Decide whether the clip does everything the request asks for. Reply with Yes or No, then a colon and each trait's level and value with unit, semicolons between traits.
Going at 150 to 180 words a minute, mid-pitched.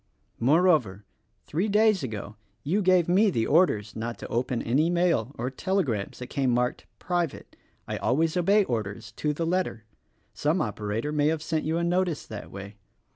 Yes: average, 170 wpm; medium, 150 Hz